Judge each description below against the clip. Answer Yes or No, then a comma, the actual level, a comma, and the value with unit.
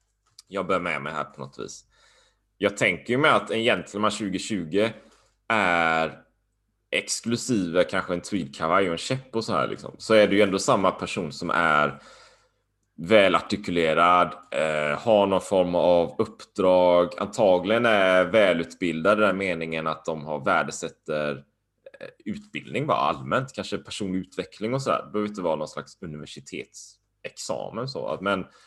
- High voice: No, very low, 95 Hz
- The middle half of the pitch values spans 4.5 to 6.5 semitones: Yes, average, 4.8 semitones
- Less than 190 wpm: Yes, average, 155 wpm